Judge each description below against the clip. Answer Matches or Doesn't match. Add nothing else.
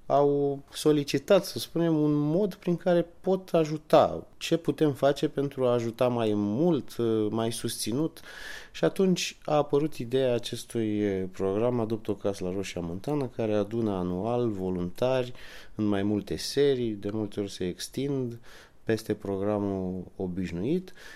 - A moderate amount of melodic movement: Doesn't match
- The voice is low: Matches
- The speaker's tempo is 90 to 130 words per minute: Doesn't match